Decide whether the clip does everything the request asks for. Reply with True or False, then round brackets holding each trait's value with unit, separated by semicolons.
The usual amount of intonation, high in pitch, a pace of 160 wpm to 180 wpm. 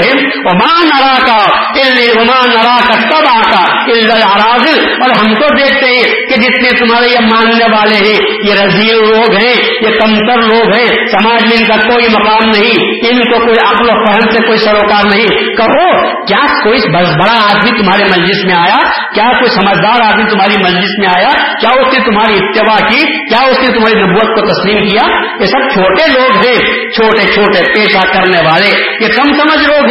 True (3.2 semitones; 225 Hz; 170 wpm)